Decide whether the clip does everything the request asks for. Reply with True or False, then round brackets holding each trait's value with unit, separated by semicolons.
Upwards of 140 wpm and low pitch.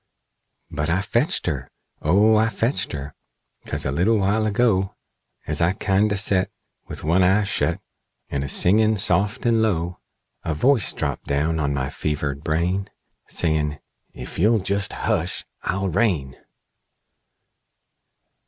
False (135 wpm; 95 Hz)